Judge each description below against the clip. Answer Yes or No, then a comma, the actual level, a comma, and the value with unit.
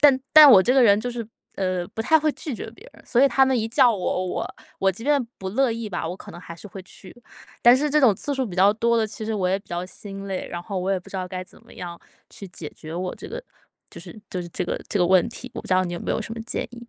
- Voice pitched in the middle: No, high, 205 Hz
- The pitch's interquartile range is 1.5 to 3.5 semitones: No, average, 4.7 semitones